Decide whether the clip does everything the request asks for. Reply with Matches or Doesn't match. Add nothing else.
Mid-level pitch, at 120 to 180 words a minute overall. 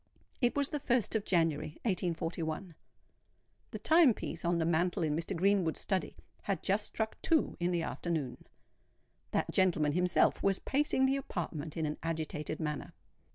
Matches